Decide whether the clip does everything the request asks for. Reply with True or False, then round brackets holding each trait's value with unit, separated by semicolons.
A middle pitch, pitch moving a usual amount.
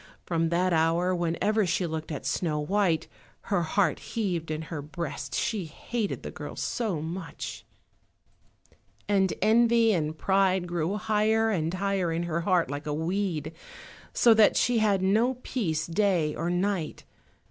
True (180 Hz; 4.1 semitones)